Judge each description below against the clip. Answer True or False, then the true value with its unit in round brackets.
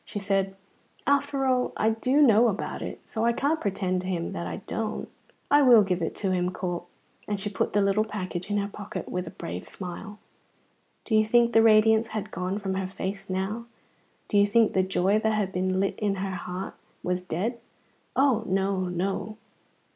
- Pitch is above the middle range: True (200 Hz)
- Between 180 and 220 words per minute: True (200 wpm)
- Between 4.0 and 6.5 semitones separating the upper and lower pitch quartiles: False (3.0 semitones)